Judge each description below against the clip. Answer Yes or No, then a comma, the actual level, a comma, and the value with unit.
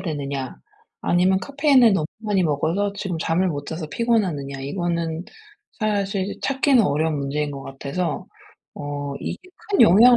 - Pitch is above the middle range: No, medium, 175 Hz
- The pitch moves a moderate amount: No, wide, 5.9 semitones